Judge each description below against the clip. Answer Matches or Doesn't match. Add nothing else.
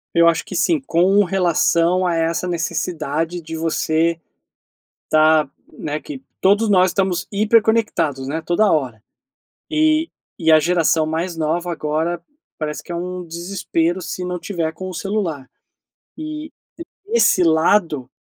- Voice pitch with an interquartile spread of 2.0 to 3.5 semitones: Matches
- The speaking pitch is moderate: Matches